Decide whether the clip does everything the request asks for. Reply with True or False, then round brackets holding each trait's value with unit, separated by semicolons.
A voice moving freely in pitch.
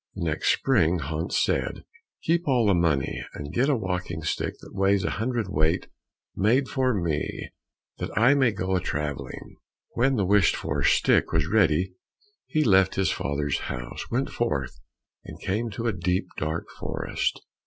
True (6.5 semitones)